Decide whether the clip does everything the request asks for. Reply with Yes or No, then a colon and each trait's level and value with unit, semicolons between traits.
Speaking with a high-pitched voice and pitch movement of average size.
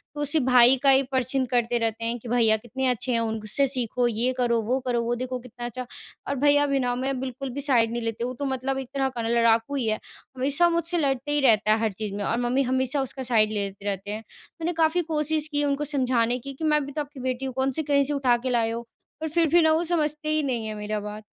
Yes: very high, 255 Hz; average, 3.4 semitones